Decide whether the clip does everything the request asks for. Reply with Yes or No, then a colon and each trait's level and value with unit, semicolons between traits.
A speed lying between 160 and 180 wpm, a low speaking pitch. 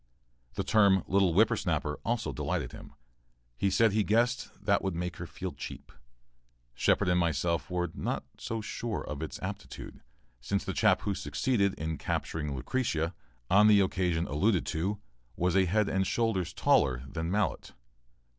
Yes: average, 165 wpm; very low, 95 Hz